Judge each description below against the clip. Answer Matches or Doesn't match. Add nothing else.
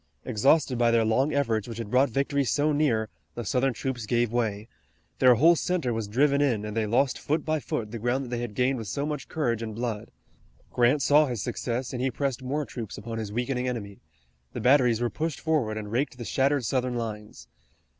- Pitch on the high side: Doesn't match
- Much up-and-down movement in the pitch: Doesn't match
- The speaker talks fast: Matches